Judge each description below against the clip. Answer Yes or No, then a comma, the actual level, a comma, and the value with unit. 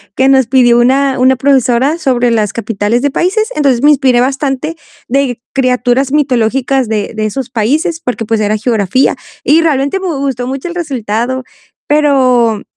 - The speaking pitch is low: No, very high, 260 Hz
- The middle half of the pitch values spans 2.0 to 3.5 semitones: Yes, average, 2.9 semitones